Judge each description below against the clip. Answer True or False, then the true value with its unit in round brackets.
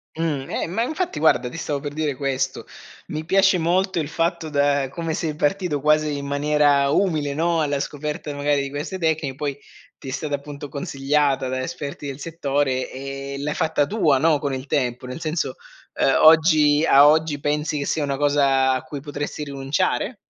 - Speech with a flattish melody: True (2.2 semitones)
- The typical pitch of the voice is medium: True (145 Hz)